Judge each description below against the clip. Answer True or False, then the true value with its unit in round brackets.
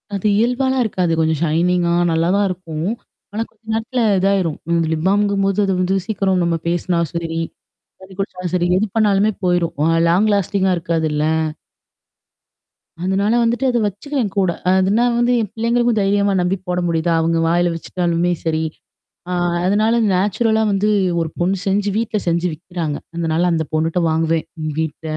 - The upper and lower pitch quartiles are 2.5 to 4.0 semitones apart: True (3.7 semitones)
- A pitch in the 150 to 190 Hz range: True (185 Hz)